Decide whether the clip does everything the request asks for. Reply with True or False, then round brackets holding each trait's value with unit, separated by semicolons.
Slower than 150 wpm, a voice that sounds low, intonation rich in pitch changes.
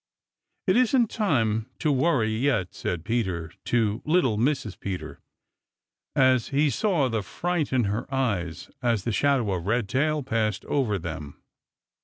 True (140 wpm; 120 Hz; 5.7 semitones)